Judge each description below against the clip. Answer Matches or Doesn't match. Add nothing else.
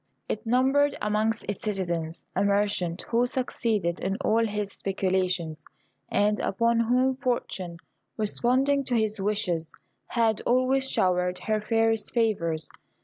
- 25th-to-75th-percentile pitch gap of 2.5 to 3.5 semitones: Doesn't match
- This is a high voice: Matches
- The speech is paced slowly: Matches